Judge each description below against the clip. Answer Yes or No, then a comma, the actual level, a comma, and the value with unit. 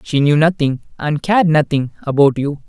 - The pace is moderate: Yes, average, 180 wpm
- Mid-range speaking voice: Yes, medium, 150 Hz